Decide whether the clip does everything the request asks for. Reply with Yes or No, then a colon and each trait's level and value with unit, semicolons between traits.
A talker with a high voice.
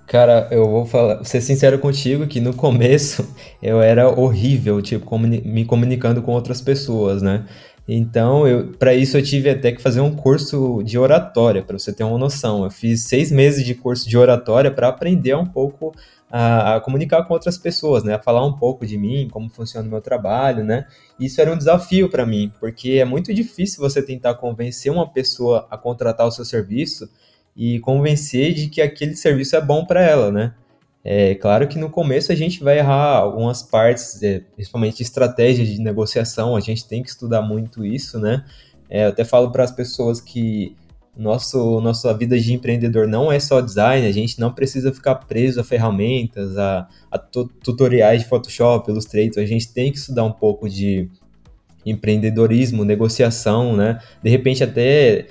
No: low, 120 Hz